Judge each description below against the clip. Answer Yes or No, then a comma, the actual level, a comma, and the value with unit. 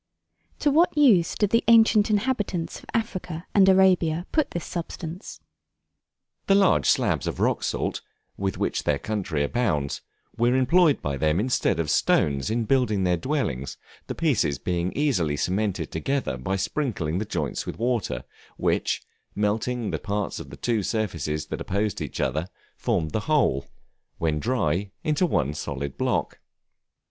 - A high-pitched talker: No, low, 110 Hz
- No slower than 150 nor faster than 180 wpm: Yes, average, 155 wpm